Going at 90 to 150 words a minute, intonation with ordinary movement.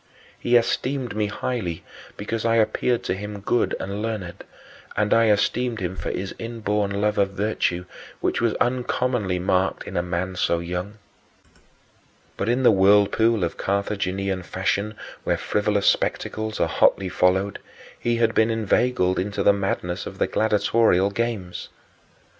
Yes: average, 145 wpm; average, 3.1 semitones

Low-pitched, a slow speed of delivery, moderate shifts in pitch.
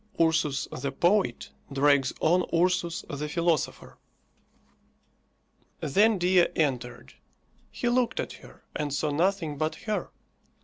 No: medium, 160 Hz; slow, 115 wpm; average, 4.0 semitones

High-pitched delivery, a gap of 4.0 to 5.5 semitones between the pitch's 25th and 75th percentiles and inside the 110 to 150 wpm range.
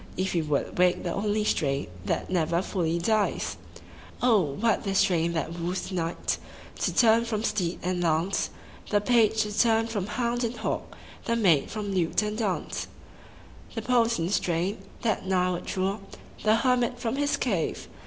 No: high, 200 Hz; average, 4.5 semitones; average, 165 wpm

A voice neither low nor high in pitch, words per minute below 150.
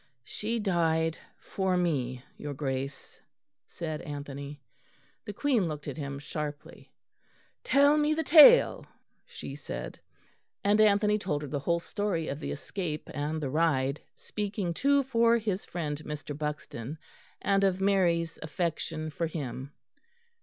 Yes: medium, 165 Hz; slow, 135 wpm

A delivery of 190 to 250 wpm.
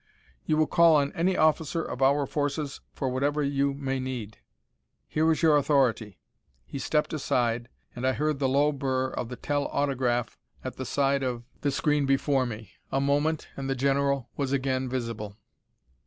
No: average, 175 wpm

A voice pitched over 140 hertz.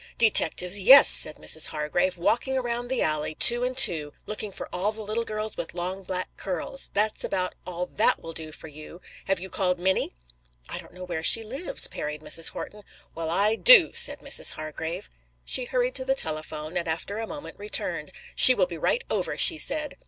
Yes: high, 190 Hz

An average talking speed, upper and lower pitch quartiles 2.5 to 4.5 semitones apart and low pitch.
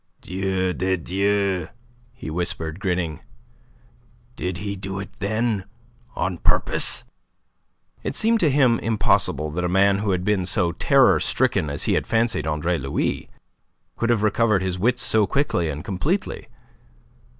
Yes: average, 145 wpm; average, 4.0 semitones; very low, 95 Hz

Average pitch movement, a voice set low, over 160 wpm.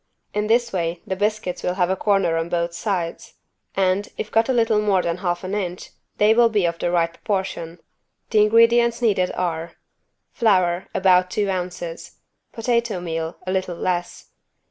No: average, 3.4 semitones; medium, 185 Hz; average, 170 wpm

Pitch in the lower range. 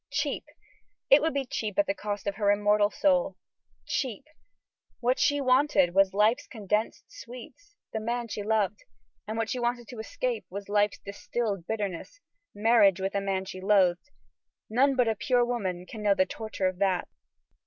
No: high, 215 Hz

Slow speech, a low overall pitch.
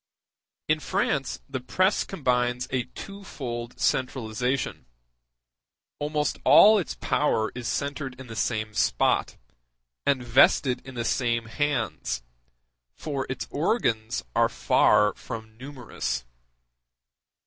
Yes: slow, 105 wpm; low, 125 Hz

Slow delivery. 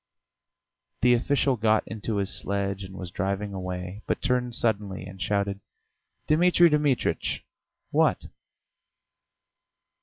Yes: slow, 110 wpm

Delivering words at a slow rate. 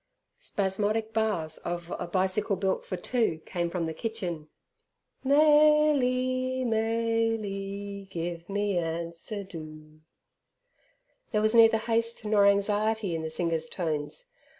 Yes: slow, 115 wpm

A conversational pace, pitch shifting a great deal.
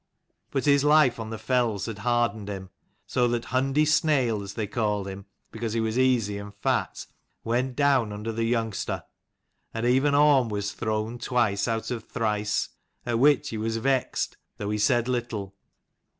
No: average, 170 wpm; average, 3.2 semitones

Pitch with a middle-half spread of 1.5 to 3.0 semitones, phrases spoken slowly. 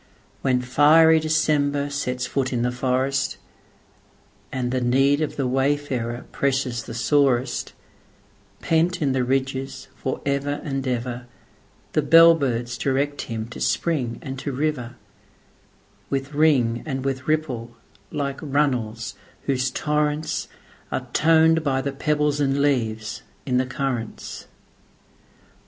Yes: narrow, 2.6 semitones; slow, 115 wpm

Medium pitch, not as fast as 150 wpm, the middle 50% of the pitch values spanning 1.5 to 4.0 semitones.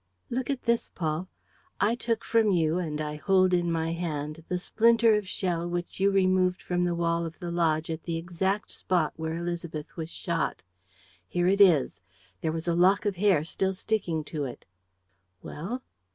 No: medium, 175 Hz; average, 180 wpm; average, 3.0 semitones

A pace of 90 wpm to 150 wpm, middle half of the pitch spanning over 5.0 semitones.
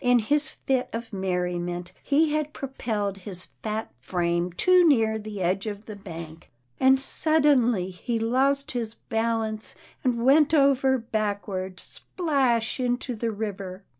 Yes: slow, 135 wpm; wide, 5.4 semitones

